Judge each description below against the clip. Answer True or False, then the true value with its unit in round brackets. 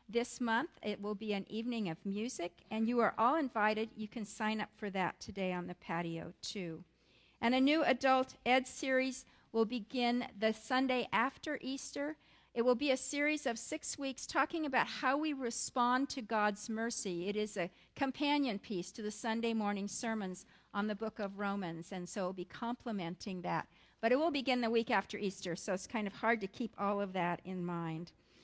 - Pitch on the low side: False (225 Hz)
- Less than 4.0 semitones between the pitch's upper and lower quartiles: False (4.3 semitones)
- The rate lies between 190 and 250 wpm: True (200 wpm)